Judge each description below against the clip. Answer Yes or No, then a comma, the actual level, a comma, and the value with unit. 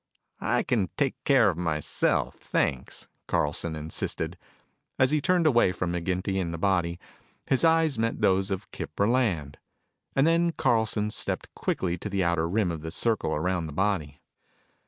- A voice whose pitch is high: No, very low, 95 Hz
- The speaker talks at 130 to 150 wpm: No, average, 160 wpm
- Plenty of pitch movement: Yes, wide, 5.8 semitones